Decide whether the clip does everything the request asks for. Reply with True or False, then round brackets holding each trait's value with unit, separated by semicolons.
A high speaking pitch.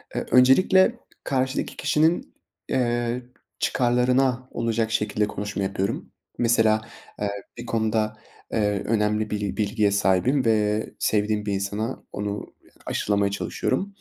False (110 Hz)